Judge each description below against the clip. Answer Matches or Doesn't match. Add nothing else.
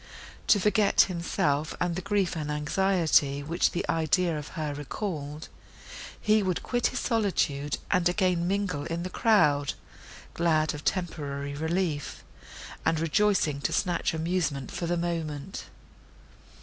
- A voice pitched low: Doesn't match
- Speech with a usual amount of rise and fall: Matches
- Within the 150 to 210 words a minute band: Doesn't match